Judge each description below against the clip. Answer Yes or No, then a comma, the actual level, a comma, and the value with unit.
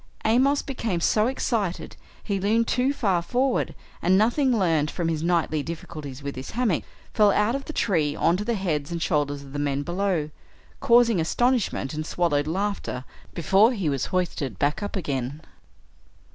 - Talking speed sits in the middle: Yes, average, 165 wpm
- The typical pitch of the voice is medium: Yes, medium, 180 Hz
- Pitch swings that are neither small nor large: No, wide, 6.8 semitones